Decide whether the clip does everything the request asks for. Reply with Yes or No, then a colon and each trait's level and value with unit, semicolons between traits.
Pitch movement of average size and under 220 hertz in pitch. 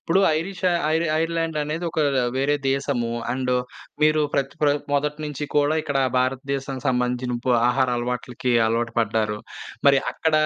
Yes: average, 3.4 semitones; low, 135 Hz